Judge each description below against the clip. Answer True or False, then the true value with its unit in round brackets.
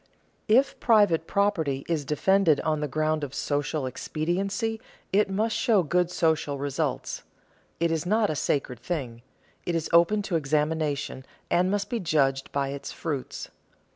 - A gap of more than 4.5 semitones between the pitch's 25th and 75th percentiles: True (5.3 semitones)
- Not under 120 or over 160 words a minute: True (155 wpm)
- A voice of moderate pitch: True (160 Hz)